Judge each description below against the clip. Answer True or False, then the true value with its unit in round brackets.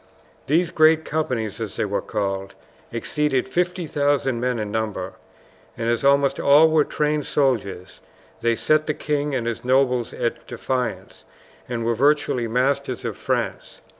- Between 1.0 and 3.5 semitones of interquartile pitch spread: False (4.2 semitones)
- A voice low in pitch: True (130 Hz)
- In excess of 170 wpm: False (145 wpm)